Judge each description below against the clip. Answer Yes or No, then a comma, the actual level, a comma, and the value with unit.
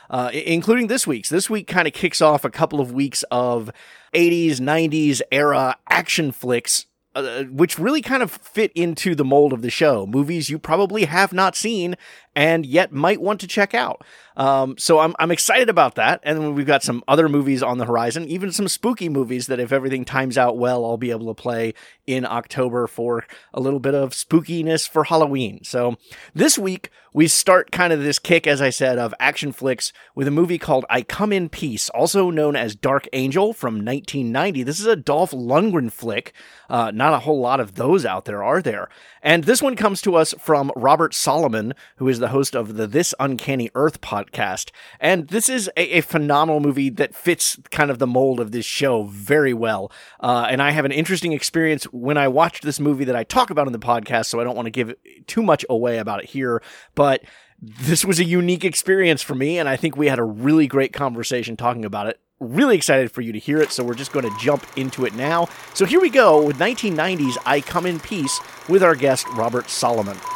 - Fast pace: Yes, fast, 215 wpm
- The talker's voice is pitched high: No, medium, 145 Hz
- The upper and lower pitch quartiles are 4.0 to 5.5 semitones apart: Yes, average, 5.2 semitones